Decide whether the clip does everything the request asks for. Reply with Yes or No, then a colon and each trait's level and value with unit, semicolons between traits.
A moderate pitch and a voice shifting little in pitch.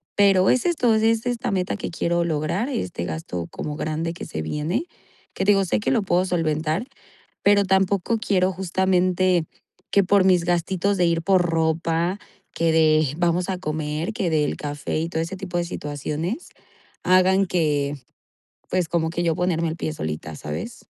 No: medium, 175 Hz; average, 3.3 semitones